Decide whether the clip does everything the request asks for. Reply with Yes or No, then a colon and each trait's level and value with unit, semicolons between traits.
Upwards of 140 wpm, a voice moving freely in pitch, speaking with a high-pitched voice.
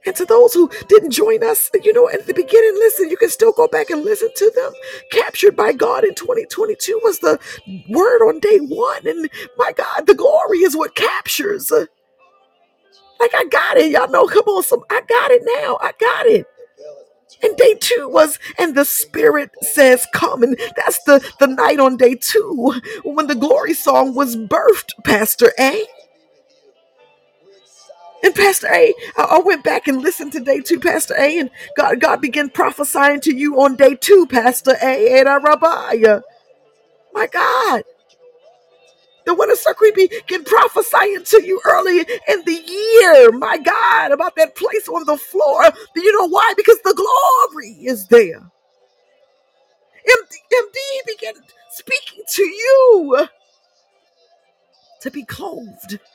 Yes: average, 160 wpm; wide, 7.2 semitones; very high, 390 Hz